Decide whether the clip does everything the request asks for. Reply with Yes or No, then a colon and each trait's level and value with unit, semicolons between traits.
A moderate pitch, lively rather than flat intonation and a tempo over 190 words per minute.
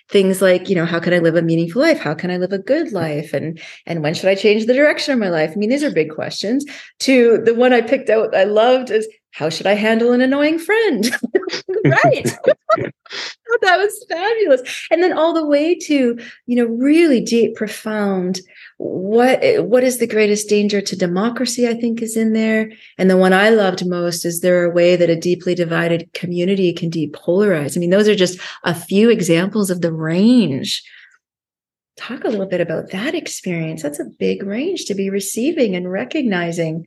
No: high, 210 Hz; wide, 6.4 semitones; average, 200 wpm